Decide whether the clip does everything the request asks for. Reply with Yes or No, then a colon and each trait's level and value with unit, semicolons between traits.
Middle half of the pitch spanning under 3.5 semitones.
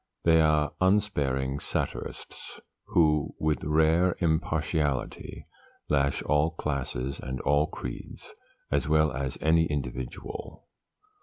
Yes: narrow, 2.6 semitones